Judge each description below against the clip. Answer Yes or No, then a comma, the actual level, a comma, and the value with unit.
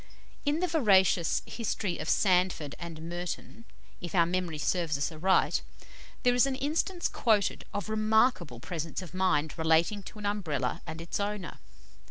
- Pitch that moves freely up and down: No, average, 4.8 semitones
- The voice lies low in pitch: No, medium, 185 Hz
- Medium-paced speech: Yes, average, 160 wpm